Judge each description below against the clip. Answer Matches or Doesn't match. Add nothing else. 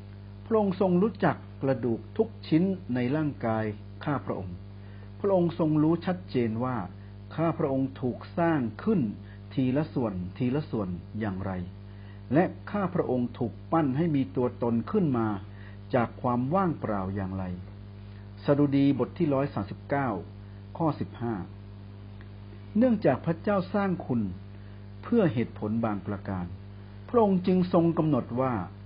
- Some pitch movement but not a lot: Doesn't match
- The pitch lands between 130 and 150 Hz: Doesn't match